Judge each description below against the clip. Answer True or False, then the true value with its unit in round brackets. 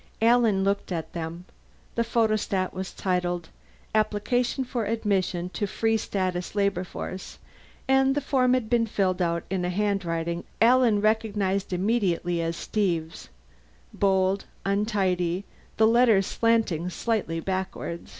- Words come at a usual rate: False (125 wpm)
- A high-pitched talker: True (195 Hz)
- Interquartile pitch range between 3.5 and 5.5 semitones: True (3.8 semitones)